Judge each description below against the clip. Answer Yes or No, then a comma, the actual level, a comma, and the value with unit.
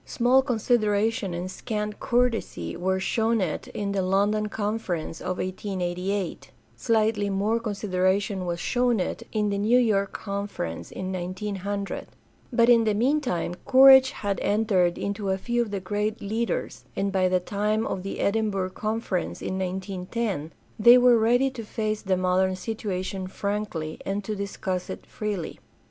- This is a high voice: Yes, high, 205 Hz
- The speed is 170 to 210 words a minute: No, average, 155 wpm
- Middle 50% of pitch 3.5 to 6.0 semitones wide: No, average, 3.0 semitones